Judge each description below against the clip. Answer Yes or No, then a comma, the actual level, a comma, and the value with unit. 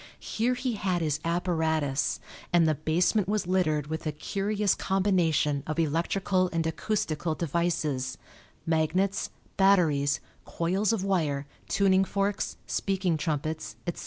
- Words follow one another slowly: Yes, slow, 125 wpm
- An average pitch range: Yes, average, 3.8 semitones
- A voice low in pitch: No, medium, 170 Hz